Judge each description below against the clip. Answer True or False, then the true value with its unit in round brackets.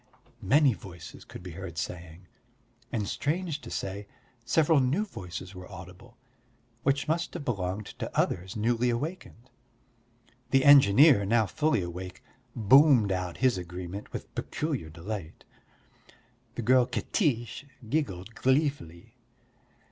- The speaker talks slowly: True (120 wpm)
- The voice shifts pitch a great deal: True (7.2 semitones)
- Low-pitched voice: True (115 Hz)